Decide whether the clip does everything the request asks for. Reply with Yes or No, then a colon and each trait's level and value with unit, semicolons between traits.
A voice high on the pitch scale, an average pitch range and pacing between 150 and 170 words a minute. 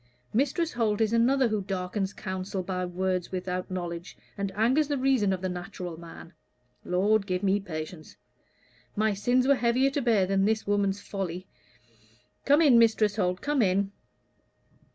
Yes: high, 200 Hz; average, 4.2 semitones; average, 155 wpm